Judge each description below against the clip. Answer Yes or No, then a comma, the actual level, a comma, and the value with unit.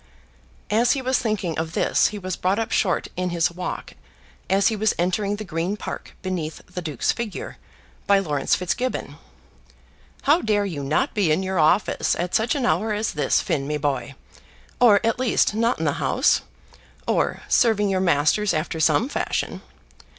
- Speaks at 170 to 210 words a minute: Yes, average, 175 wpm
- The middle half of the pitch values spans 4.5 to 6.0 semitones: Yes, average, 4.9 semitones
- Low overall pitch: No, high, 190 Hz